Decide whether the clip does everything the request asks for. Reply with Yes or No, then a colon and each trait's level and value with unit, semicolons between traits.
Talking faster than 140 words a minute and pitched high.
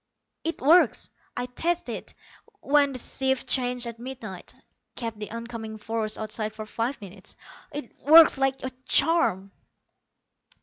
No: slow, 135 wpm; high, 245 Hz